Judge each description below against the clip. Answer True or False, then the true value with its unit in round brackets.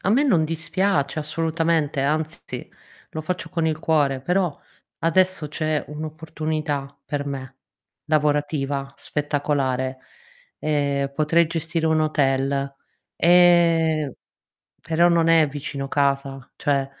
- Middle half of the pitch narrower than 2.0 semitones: False (2.7 semitones)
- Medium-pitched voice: True (155 Hz)